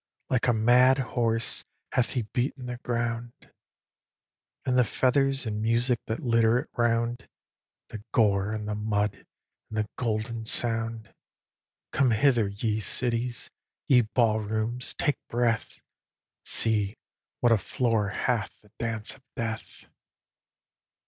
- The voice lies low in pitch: Yes, low, 115 Hz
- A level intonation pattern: Yes, narrow, 2.1 semitones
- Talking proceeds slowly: Yes, slow, 130 wpm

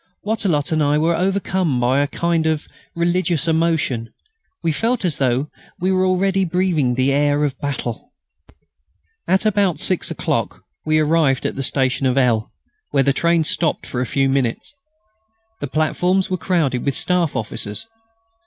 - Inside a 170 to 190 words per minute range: No, average, 160 wpm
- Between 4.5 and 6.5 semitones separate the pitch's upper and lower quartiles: Yes, average, 4.8 semitones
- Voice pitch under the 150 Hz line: No, medium, 155 Hz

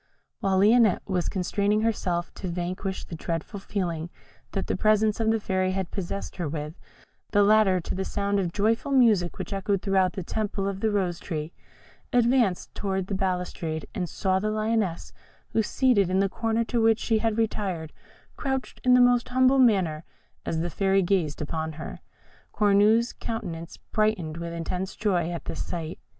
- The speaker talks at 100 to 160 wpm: No, average, 175 wpm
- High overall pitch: Yes, high, 195 Hz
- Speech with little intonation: No, average, 3.8 semitones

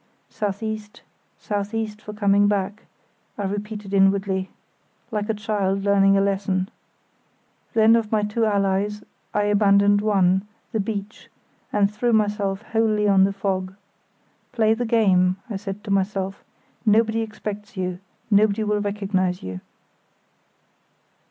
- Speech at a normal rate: No, slow, 130 wpm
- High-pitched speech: Yes, high, 205 Hz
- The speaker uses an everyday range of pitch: No, narrow, 1.5 semitones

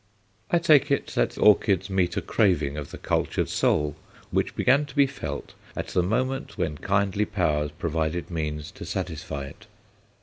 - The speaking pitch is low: Yes, very low, 90 Hz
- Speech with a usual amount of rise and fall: No, wide, 6.6 semitones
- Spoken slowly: No, average, 165 wpm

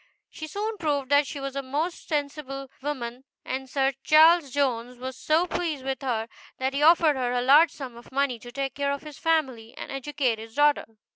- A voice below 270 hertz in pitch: No, very high, 275 Hz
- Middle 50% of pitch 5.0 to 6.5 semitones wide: No, average, 2.7 semitones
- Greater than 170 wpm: Yes, fast, 205 wpm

